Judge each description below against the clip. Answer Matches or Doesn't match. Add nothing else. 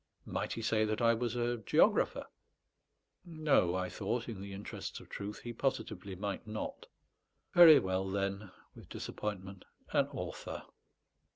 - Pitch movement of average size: Matches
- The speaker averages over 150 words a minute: Doesn't match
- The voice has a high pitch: Doesn't match